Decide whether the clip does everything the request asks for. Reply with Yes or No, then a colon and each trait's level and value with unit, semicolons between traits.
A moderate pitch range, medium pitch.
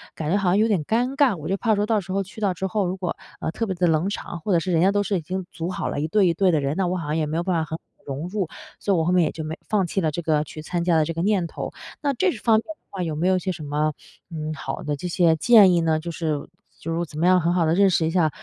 Yes: average, 3.5 semitones; medium, 175 Hz